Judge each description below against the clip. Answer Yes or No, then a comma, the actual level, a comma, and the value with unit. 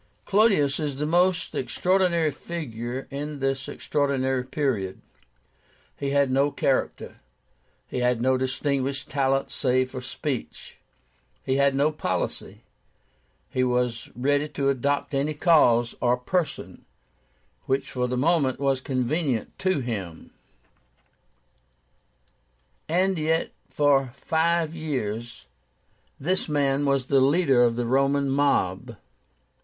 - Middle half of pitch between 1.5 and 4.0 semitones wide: Yes, average, 2.9 semitones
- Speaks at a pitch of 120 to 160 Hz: Yes, medium, 140 Hz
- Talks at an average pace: No, slow, 115 wpm